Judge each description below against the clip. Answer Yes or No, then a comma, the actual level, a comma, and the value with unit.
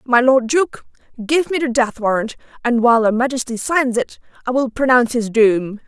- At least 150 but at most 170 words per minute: No, average, 195 wpm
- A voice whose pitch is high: Yes, high, 245 Hz